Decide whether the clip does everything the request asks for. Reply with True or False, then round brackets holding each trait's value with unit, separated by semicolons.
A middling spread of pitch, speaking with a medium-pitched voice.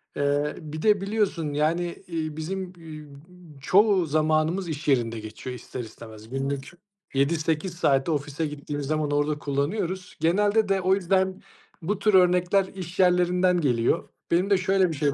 True (4.3 semitones; 160 Hz)